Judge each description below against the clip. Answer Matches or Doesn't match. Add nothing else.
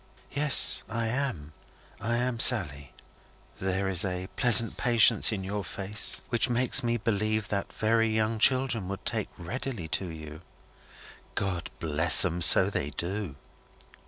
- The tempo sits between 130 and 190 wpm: Matches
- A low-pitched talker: Matches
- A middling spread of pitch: Matches